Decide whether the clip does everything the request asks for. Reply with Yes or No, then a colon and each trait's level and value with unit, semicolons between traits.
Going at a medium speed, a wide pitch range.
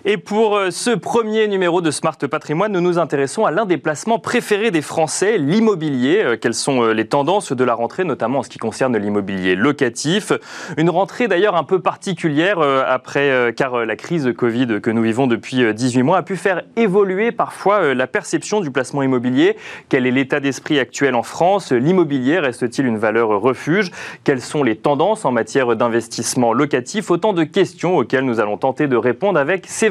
Yes: average, 185 wpm; wide, 7.8 semitones